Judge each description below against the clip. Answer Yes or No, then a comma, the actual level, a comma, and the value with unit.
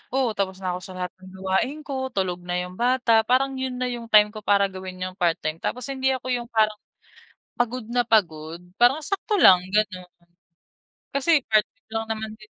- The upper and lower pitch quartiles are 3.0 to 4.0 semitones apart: No, average, 5.1 semitones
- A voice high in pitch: Yes, high, 215 Hz